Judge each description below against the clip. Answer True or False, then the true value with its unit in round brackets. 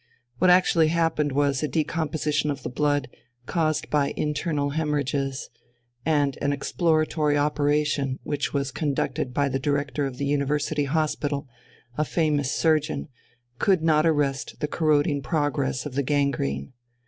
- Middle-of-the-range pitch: True (145 Hz)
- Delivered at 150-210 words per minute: False (135 wpm)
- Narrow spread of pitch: True (1.7 semitones)